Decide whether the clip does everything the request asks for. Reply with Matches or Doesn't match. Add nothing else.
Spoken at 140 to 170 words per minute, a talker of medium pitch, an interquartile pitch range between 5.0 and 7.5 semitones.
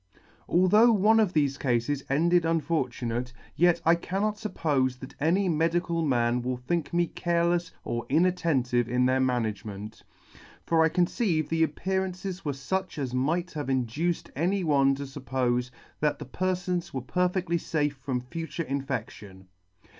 Matches